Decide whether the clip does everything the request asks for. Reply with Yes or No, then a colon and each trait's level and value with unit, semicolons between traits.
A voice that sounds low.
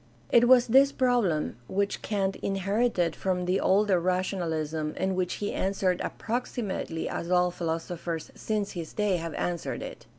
No: medium, 185 Hz